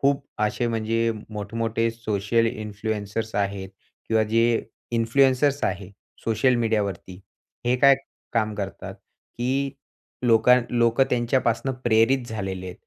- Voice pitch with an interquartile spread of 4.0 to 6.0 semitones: No, narrow, 2.4 semitones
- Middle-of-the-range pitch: No, low, 115 Hz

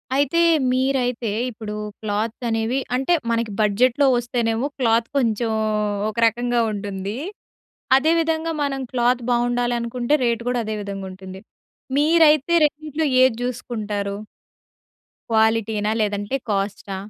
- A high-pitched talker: Yes, high, 235 Hz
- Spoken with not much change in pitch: No, average, 3.2 semitones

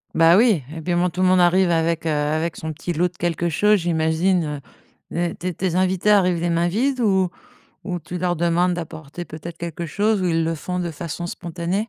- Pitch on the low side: No, medium, 175 Hz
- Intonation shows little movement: Yes, narrow, 1.9 semitones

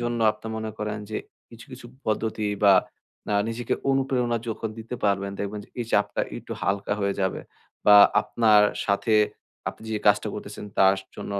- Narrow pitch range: Yes, narrow, 2.3 semitones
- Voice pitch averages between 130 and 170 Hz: No, low, 110 Hz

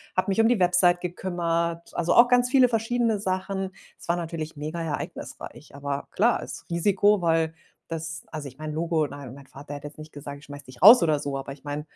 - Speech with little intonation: No, average, 4.4 semitones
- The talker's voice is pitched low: No, medium, 165 Hz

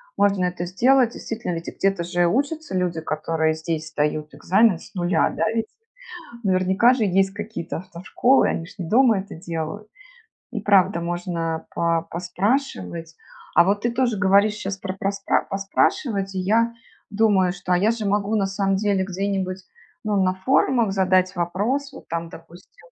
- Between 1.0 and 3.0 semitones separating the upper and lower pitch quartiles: No, average, 3.4 semitones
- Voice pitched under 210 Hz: Yes, high, 190 Hz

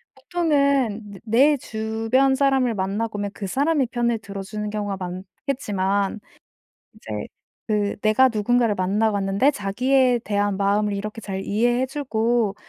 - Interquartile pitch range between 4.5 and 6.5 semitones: No, average, 3.7 semitones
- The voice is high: Yes, high, 220 Hz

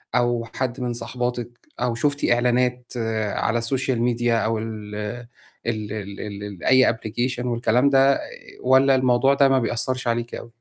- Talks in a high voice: No, low, 120 Hz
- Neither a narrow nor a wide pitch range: No, narrow, 1.9 semitones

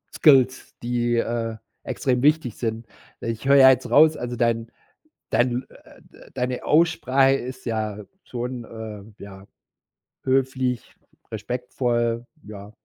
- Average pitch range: No, narrow, 2.3 semitones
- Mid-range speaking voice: No, low, 120 Hz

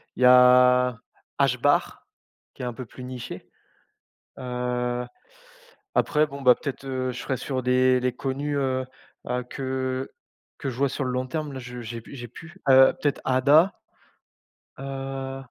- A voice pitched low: Yes, low, 130 Hz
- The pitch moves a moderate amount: No, narrow, 1.3 semitones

